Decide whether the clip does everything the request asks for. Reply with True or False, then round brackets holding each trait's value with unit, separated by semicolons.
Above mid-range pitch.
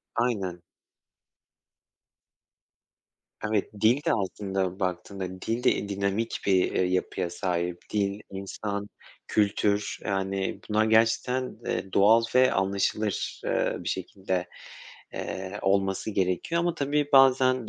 False (100 Hz)